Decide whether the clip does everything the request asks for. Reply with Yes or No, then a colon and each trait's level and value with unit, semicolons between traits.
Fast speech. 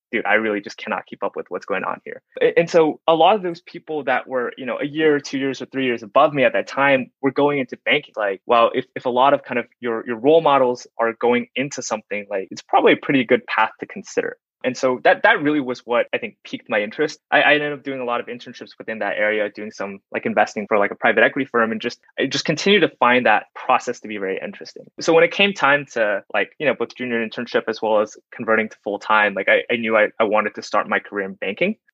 Yes: fast, 270 wpm